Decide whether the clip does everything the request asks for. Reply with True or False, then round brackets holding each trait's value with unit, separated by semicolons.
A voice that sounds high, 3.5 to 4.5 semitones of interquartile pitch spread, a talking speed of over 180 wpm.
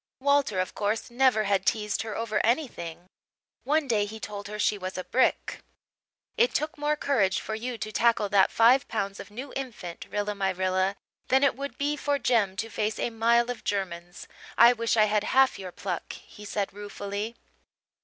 True (215 Hz; 3.9 semitones; 190 wpm)